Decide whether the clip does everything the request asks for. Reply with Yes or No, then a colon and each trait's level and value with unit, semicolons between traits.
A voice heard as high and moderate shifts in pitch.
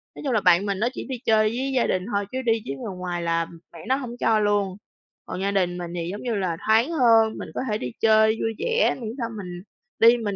Yes: high, 215 Hz; average, 4.1 semitones